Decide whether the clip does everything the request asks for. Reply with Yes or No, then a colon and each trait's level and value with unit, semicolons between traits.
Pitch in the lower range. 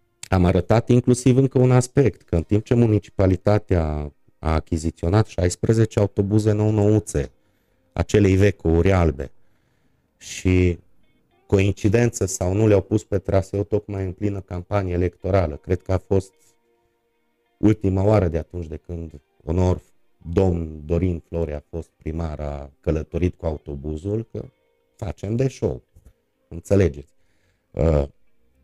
Yes: very low, 95 Hz